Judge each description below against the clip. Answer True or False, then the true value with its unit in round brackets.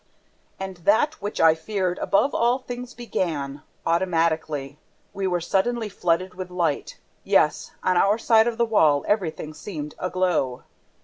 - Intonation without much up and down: False (4.9 semitones)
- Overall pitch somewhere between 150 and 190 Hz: True (185 Hz)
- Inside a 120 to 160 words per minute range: True (140 wpm)